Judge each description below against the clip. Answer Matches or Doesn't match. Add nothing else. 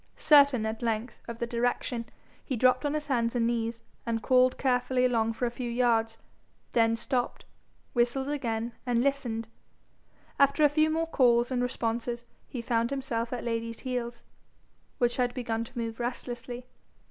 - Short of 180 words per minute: Matches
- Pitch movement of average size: Doesn't match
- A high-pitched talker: Matches